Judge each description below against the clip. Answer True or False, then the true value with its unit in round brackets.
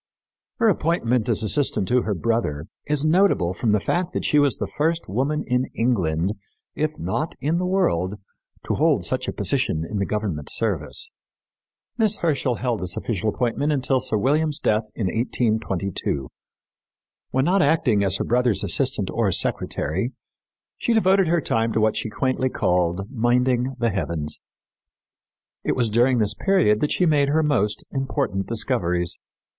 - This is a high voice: False (120 Hz)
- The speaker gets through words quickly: False (160 wpm)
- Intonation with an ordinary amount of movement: False (6.4 semitones)